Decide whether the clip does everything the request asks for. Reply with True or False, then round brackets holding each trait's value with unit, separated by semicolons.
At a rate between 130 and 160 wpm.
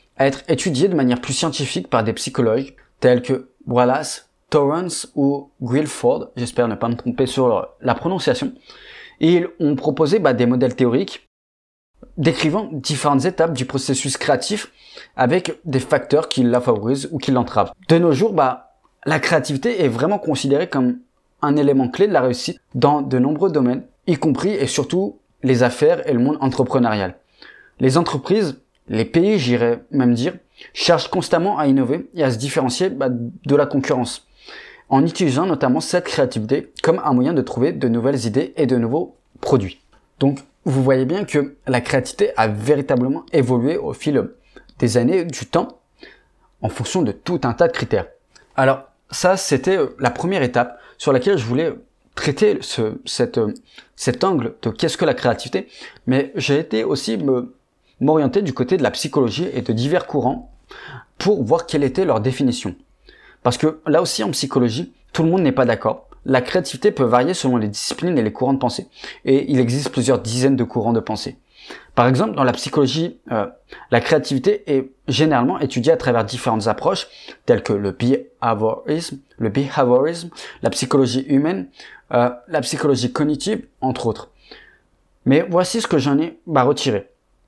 False (170 wpm)